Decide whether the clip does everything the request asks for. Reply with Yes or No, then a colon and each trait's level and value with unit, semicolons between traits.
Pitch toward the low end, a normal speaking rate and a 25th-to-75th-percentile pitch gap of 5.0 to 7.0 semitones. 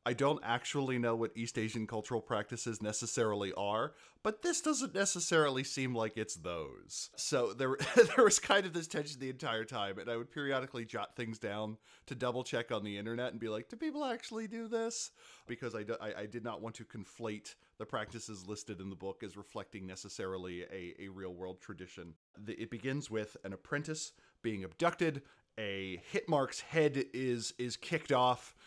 Yes: low, 115 Hz; average, 185 wpm; average, 5.3 semitones